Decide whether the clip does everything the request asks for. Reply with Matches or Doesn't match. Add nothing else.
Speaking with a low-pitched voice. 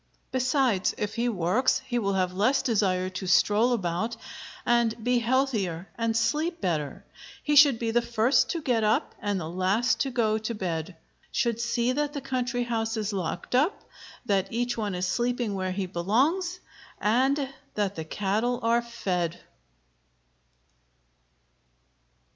Doesn't match